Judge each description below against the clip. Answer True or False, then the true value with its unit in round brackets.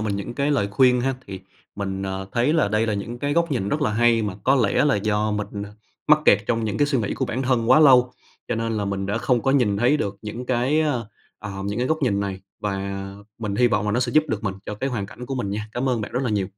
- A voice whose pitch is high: False (115 Hz)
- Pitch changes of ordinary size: True (4.0 semitones)